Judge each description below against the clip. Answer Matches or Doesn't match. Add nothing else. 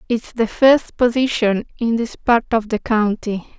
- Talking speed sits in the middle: Matches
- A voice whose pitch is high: Matches